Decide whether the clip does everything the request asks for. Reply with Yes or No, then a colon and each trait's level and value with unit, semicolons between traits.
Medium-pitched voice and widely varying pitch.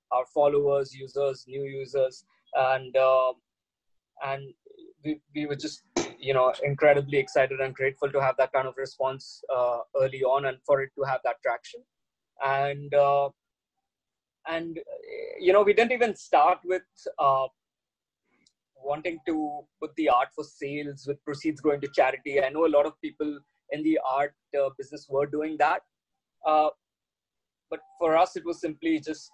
No: medium, 145 Hz; average, 2.9 semitones